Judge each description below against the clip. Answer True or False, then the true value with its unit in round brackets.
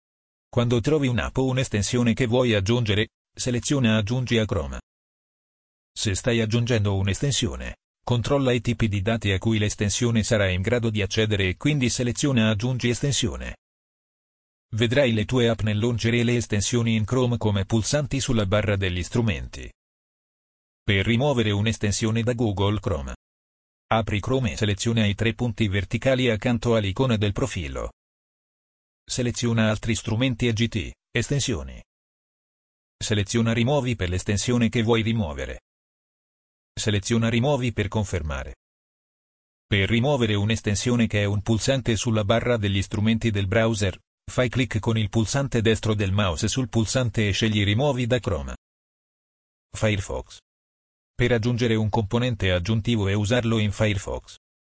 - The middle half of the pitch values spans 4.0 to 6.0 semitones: False (3.3 semitones)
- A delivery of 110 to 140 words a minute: True (135 wpm)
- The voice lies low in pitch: True (110 Hz)